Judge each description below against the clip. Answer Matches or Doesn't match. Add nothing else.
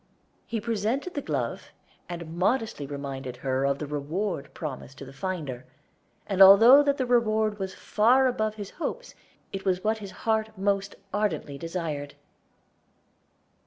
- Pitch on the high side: Matches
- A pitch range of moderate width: Doesn't match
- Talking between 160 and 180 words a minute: Doesn't match